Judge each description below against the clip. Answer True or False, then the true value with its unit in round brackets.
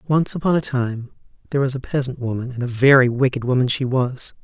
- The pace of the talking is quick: True (215 wpm)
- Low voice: True (130 Hz)